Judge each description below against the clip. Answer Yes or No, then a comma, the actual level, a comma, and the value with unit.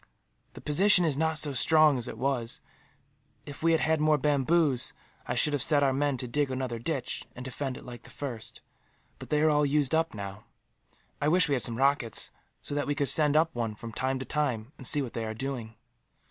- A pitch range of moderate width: Yes, average, 3.3 semitones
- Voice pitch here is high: No, medium, 140 Hz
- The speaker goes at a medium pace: No, fast, 225 wpm